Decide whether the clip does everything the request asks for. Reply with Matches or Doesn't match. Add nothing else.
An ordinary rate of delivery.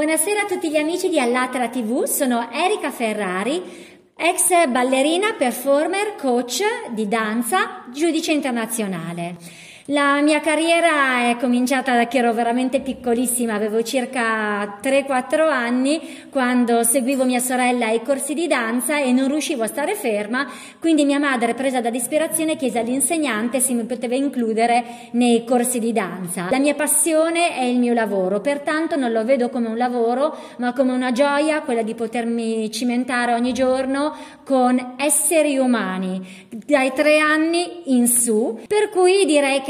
Matches